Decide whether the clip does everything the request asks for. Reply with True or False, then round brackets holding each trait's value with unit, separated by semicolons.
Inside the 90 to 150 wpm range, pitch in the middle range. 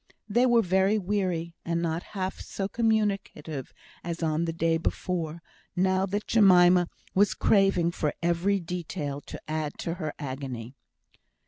True (140 wpm; 175 Hz)